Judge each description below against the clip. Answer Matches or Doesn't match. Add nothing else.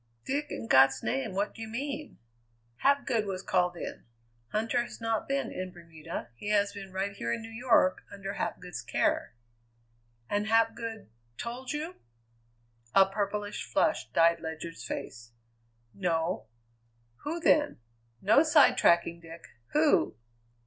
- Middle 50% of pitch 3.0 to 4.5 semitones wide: Doesn't match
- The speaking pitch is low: Doesn't match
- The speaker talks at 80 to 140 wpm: Matches